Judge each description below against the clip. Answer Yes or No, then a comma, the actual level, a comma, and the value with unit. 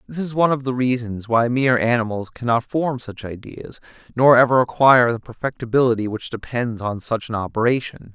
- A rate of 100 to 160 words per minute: No, average, 175 wpm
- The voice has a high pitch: No, low, 120 Hz